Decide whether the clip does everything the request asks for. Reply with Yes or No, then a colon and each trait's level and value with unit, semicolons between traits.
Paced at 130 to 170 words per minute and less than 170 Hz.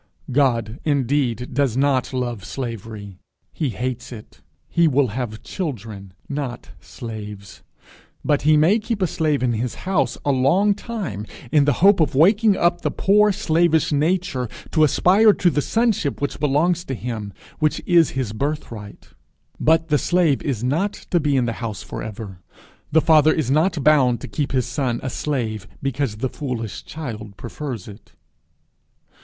Yes: average, 160 wpm; medium, 140 Hz